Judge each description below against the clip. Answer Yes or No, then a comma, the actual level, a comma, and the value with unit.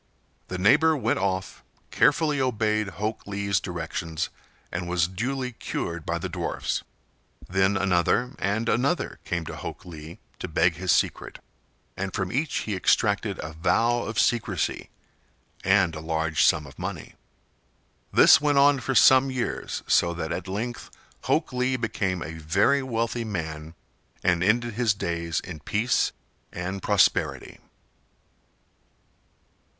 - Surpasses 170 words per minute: No, slow, 135 wpm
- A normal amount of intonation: No, wide, 5.8 semitones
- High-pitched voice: No, low, 100 Hz